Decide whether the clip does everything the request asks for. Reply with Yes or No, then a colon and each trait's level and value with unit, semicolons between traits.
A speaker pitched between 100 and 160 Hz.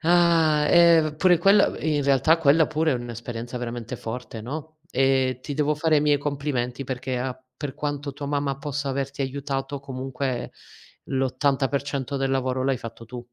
Yes: medium, 140 Hz